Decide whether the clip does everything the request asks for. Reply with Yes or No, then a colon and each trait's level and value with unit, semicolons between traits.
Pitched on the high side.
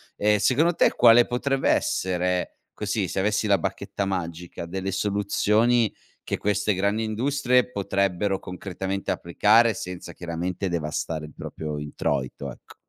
No: low, 100 Hz